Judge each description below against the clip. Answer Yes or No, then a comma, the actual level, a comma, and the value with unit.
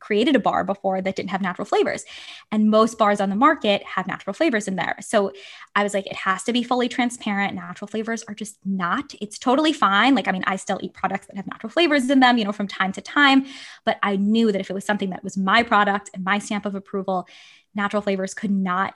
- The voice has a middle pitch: No, high, 205 Hz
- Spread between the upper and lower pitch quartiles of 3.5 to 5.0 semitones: No, average, 2.8 semitones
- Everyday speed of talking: No, fast, 245 wpm